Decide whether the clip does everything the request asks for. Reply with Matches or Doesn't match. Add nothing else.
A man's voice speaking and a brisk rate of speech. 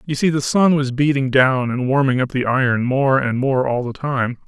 Matches